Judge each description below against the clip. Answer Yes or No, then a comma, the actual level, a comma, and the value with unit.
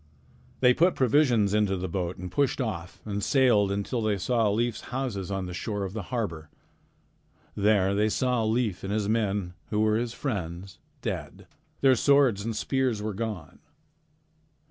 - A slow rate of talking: No, average, 165 wpm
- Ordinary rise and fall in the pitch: Yes, average, 3.8 semitones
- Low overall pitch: Yes, low, 105 Hz